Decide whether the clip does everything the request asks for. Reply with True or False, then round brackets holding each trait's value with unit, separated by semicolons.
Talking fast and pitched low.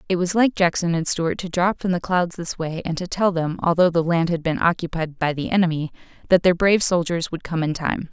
False (250 wpm; 170 Hz)